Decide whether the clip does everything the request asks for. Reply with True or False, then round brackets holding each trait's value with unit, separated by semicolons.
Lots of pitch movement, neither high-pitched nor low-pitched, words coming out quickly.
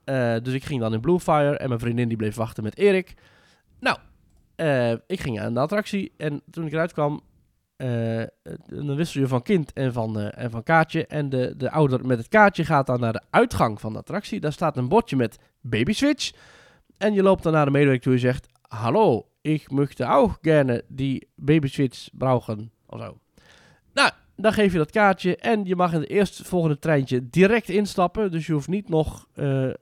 True (5.9 semitones; 145 Hz; 205 wpm)